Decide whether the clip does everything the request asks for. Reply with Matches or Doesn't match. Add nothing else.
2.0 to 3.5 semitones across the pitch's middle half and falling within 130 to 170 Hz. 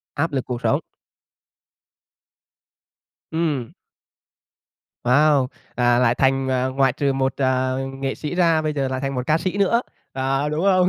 Matches